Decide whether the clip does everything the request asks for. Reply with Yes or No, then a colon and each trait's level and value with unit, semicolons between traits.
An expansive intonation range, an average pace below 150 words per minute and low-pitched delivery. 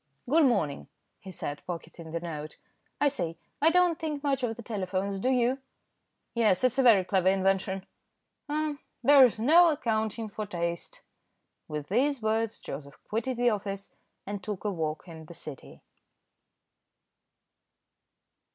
No: wide, 6.2 semitones; average, 140 wpm; high, 210 Hz